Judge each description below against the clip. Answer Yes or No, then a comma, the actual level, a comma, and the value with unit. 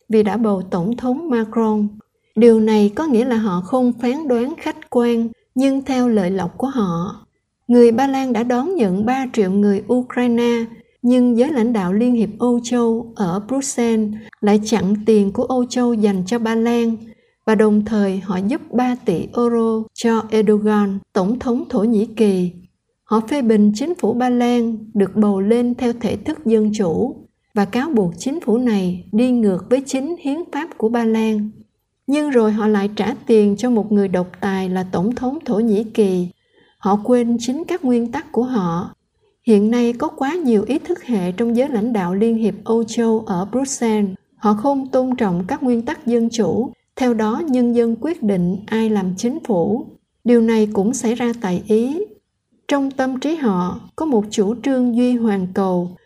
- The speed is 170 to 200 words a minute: Yes, average, 190 wpm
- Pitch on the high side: Yes, high, 230 Hz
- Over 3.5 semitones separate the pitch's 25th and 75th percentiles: No, average, 2.9 semitones